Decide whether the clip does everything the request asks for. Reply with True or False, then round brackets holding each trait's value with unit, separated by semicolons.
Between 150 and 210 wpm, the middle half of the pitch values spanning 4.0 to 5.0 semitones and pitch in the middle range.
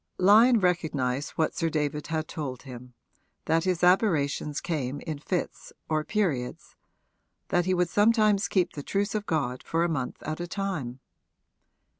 True (155 wpm; 4.5 semitones; 165 Hz)